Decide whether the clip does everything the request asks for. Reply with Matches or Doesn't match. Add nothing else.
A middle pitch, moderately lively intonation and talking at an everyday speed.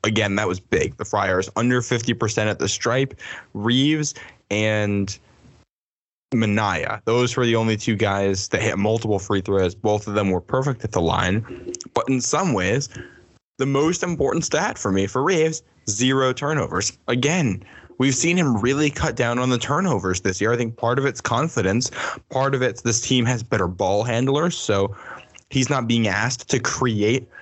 Doesn't match